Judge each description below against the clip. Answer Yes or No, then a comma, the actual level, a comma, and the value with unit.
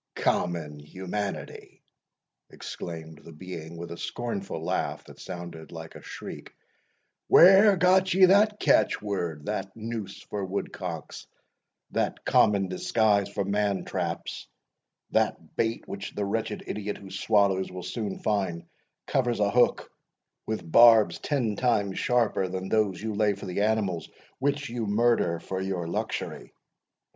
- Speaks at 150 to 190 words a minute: No, slow, 135 wpm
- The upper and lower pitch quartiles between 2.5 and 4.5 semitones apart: Yes, average, 3.7 semitones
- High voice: No, low, 100 Hz